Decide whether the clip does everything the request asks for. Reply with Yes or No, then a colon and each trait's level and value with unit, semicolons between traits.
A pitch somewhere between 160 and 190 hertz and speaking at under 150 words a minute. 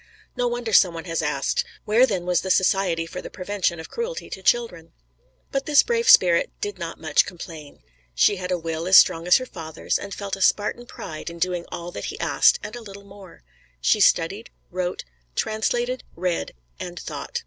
No: medium, 185 Hz; average, 195 wpm